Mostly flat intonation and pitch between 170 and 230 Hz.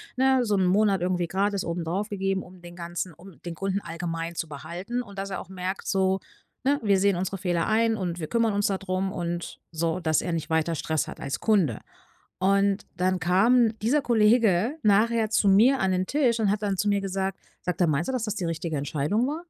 No: average, 3.5 semitones; high, 190 Hz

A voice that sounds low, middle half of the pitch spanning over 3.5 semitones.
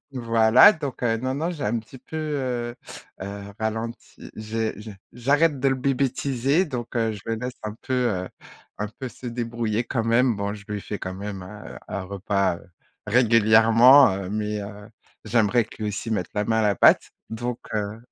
No: low, 115 Hz; average, 3.2 semitones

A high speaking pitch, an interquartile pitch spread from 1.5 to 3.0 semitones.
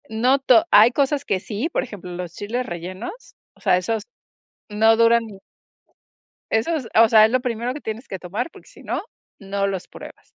No: high, 220 Hz; average, 3.8 semitones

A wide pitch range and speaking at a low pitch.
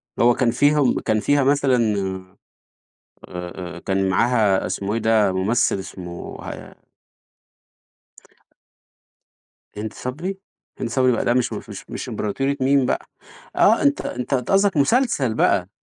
Yes: wide, 5.9 semitones; low, 120 Hz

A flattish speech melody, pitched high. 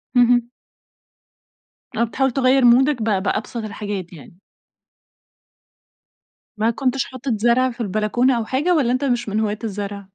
No: average, 3.5 semitones; high, 235 Hz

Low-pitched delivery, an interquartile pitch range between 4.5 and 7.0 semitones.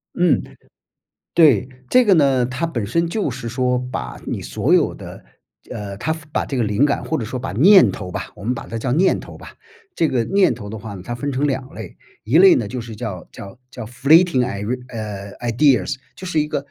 Yes: low, 125 Hz; wide, 5.4 semitones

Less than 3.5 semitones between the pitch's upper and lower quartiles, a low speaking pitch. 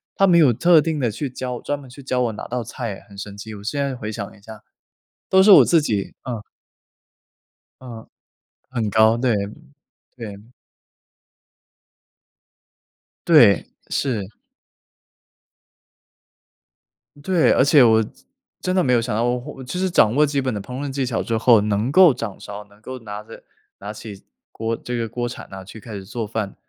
No: average, 4.0 semitones; low, 120 Hz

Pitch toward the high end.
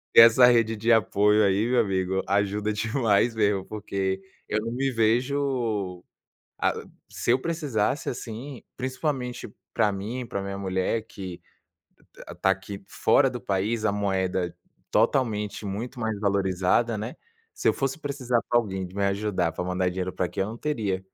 No: low, 105 Hz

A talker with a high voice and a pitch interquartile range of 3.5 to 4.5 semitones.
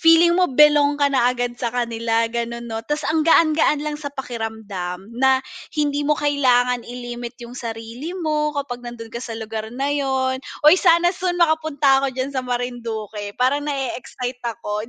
Yes: very high, 255 Hz; average, 3.9 semitones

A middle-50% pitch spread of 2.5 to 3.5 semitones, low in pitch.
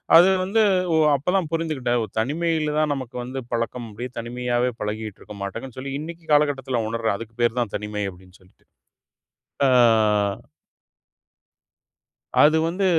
No: average, 5.3 semitones; low, 125 Hz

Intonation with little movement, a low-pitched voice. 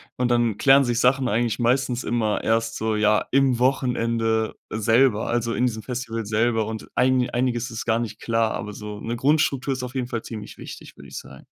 Yes: narrow, 2.1 semitones; low, 120 Hz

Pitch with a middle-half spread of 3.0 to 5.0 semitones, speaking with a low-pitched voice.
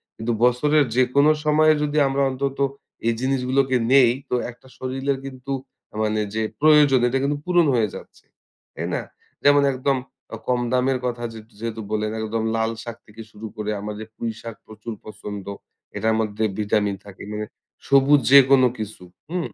Yes: average, 3.9 semitones; low, 125 Hz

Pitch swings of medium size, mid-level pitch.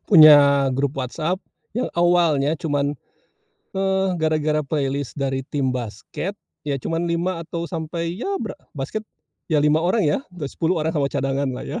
Yes: average, 3.6 semitones; medium, 155 Hz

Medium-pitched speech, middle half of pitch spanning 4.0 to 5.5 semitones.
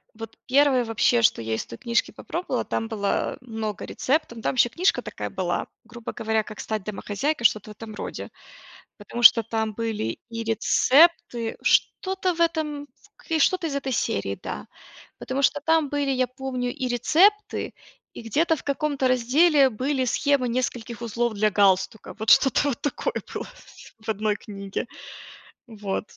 No: high, 240 Hz; average, 4.6 semitones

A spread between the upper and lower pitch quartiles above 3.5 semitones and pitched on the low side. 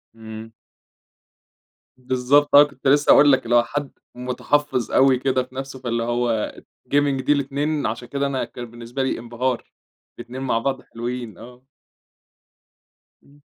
No: average, 2.7 semitones; low, 130 Hz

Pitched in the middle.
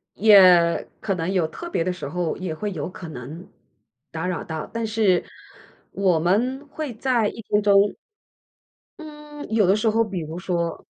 No: high, 195 Hz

